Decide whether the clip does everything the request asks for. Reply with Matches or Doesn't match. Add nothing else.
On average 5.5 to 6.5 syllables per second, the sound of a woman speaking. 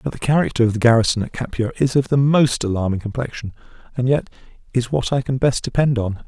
Doesn't match